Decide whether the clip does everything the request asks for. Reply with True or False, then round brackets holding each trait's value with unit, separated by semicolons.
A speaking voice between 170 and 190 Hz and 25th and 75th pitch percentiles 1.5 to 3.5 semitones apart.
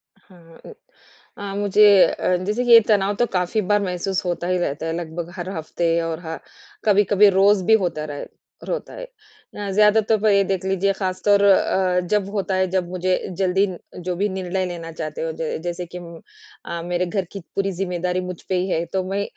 True (185 Hz; 2.5 semitones)